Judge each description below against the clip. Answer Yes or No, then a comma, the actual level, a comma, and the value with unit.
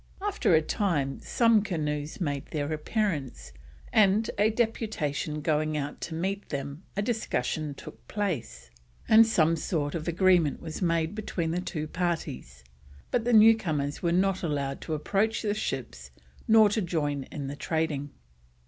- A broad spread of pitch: Yes, wide, 5.8 semitones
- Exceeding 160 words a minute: No, average, 155 wpm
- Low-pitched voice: No, medium, 160 Hz